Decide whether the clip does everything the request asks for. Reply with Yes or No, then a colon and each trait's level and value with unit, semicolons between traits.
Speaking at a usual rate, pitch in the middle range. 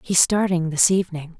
Yes: average, 170 wpm; medium, 175 Hz